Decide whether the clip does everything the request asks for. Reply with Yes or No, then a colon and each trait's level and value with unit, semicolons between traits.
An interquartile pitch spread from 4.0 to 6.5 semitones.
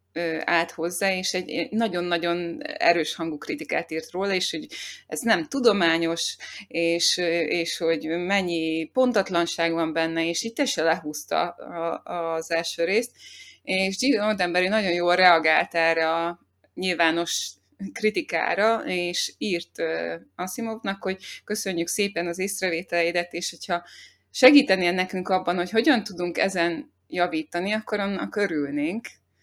No: average, 2.8 semitones